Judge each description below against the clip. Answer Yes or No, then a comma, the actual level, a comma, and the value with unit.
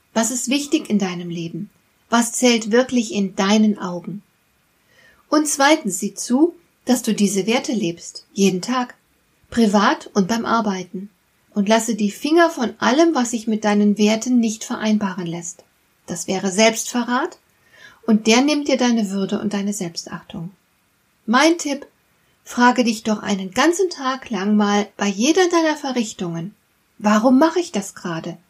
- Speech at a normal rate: Yes, average, 150 wpm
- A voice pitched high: Yes, high, 220 Hz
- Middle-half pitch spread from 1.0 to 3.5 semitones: No, average, 4.1 semitones